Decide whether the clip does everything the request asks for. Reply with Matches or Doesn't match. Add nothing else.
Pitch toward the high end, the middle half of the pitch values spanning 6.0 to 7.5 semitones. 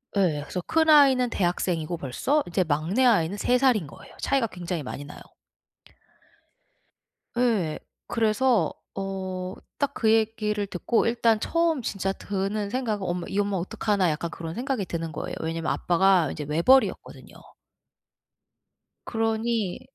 Doesn't match